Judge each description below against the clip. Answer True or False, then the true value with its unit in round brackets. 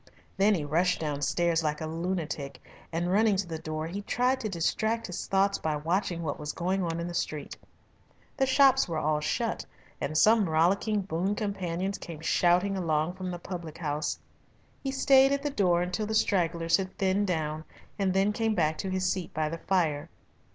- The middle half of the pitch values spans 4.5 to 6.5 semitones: False (3.8 semitones)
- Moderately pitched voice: True (180 Hz)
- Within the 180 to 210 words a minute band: True (190 wpm)